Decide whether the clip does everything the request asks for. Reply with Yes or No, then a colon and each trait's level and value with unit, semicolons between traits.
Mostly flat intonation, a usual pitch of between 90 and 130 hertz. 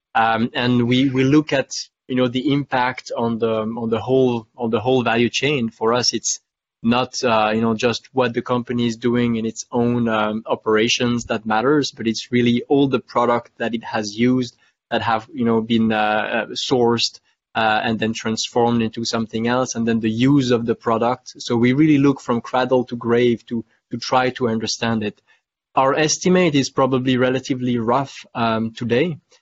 Yes: narrow, 2.0 semitones; low, 120 Hz